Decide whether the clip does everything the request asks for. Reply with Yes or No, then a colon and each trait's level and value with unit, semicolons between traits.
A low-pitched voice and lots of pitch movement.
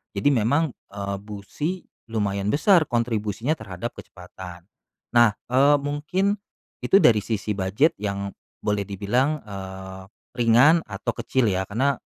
Yes: low, 110 Hz; wide, 6.1 semitones